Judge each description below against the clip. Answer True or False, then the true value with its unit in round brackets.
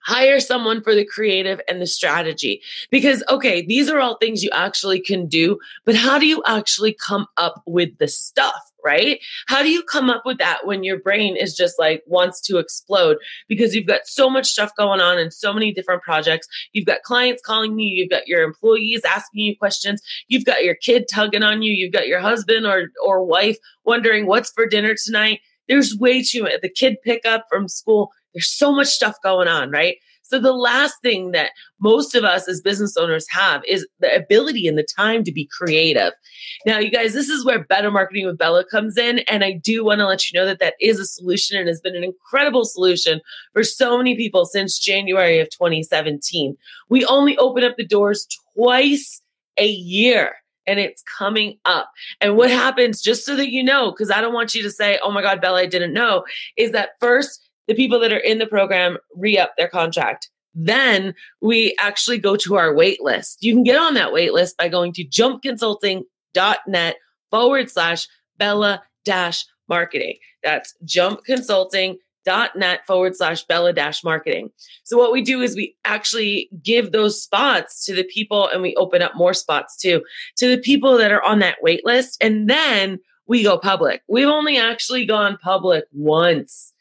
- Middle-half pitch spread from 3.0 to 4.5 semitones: False (5.0 semitones)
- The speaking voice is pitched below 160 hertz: False (210 Hz)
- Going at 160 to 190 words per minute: False (200 wpm)